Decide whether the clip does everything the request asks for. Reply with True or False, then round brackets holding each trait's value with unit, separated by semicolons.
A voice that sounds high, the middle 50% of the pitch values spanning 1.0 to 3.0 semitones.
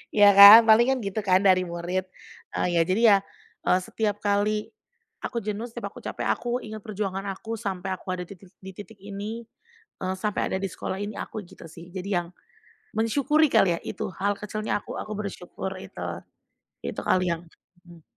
True (200 Hz; 2.7 semitones)